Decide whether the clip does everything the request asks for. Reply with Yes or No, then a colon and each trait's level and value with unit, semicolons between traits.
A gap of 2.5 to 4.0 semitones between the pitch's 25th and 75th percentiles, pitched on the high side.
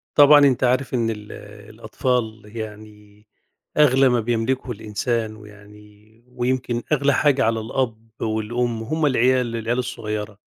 No: average, 2.9 semitones; low, 115 Hz